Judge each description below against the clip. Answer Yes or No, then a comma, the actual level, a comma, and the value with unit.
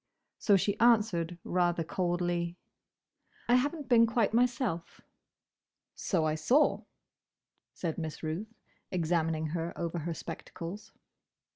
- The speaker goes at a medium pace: No, slow, 115 wpm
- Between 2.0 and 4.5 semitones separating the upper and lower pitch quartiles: No, average, 5.2 semitones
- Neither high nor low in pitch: Yes, medium, 175 Hz